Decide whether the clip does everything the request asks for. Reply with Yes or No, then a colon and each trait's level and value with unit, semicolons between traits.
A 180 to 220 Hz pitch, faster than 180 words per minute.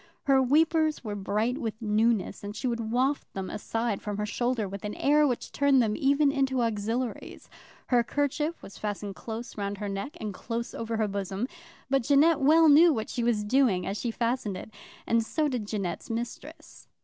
No: high, 235 Hz; average, 190 wpm